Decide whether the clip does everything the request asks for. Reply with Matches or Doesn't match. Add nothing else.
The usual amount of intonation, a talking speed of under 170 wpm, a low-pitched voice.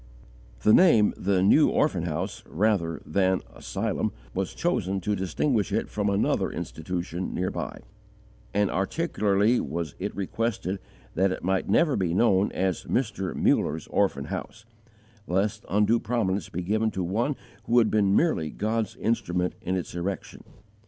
Matches